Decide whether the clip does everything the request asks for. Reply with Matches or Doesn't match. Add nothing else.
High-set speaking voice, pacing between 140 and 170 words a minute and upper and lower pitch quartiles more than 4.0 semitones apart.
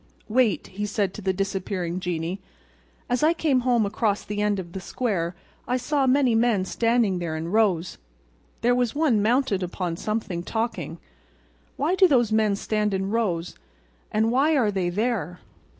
Matches